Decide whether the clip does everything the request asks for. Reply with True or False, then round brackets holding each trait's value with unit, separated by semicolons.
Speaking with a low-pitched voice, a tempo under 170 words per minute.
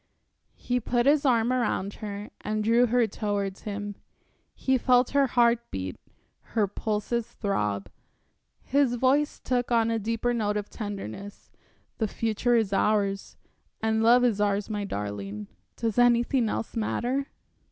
False (225 Hz; 140 wpm)